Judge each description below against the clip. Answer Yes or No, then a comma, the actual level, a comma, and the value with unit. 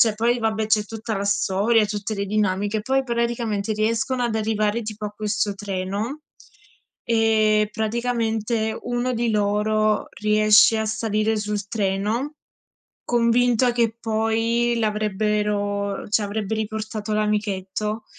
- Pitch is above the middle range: Yes, high, 215 Hz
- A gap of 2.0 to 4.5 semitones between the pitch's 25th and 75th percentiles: No, narrow, 1.5 semitones